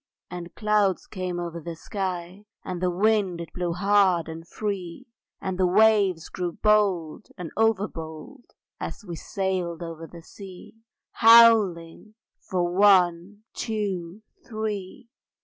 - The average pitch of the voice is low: No, medium, 185 Hz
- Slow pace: Yes, slow, 130 wpm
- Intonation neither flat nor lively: Yes, average, 3.3 semitones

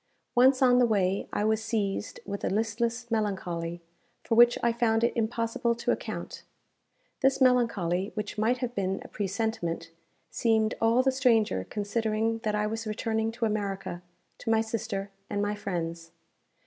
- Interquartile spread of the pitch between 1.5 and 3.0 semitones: Yes, average, 2.7 semitones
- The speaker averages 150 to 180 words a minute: Yes, average, 160 wpm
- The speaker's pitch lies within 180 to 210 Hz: No, high, 220 Hz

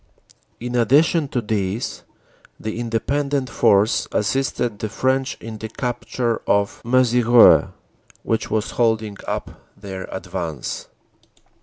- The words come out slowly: Yes, slow, 110 wpm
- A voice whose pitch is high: No, low, 115 Hz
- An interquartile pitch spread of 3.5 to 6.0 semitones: No, average, 3.1 semitones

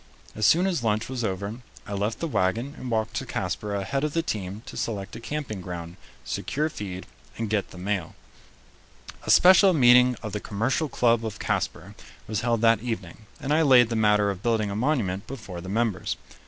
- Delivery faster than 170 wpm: Yes, average, 195 wpm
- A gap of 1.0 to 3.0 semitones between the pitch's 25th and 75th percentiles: No, average, 3.8 semitones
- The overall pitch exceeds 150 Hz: No, low, 110 Hz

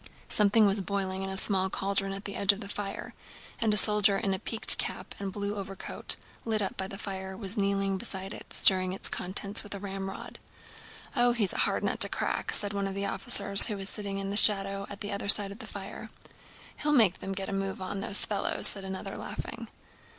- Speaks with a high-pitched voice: Yes, high, 200 Hz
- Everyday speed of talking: No, fast, 225 wpm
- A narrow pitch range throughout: Yes, narrow, 1.0 semitones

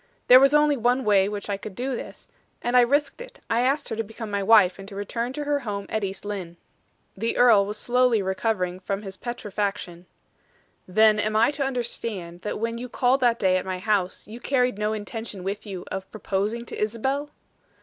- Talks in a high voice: Yes, high, 215 Hz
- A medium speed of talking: No, fast, 210 wpm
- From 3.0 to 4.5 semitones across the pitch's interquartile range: Yes, average, 3.8 semitones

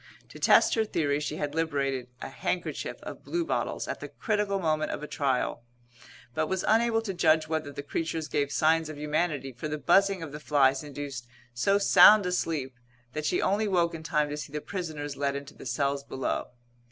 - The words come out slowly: No, average, 200 wpm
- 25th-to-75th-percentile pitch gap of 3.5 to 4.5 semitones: Yes, average, 3.8 semitones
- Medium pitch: Yes, medium, 155 Hz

